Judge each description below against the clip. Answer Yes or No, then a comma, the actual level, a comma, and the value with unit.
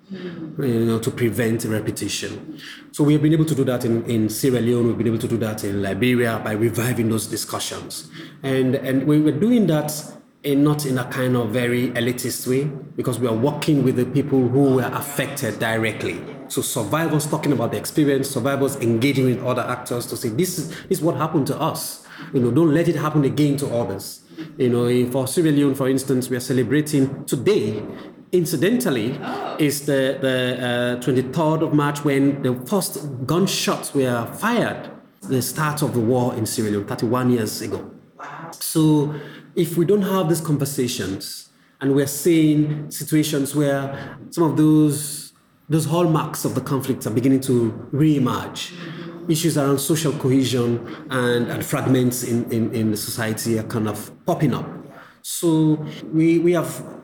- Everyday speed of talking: Yes, average, 175 wpm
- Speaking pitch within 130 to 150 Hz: Yes, low, 135 Hz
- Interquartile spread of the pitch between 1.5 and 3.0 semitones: No, average, 3.9 semitones